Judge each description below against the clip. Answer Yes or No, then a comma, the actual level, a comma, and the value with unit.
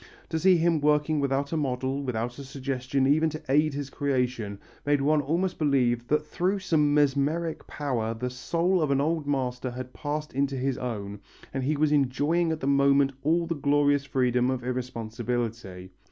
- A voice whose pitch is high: No, medium, 140 Hz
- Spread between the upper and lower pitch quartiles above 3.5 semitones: No, average, 3.1 semitones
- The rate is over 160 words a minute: Yes, average, 180 wpm